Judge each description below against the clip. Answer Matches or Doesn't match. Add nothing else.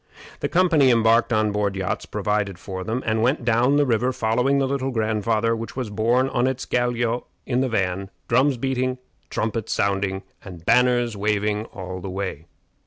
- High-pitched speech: Doesn't match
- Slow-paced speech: Doesn't match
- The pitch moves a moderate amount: Matches